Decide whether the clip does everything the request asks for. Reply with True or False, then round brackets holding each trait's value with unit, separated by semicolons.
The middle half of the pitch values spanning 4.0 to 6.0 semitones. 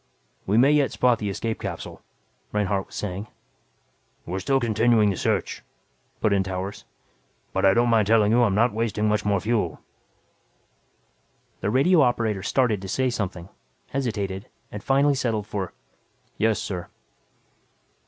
False (3.4 semitones)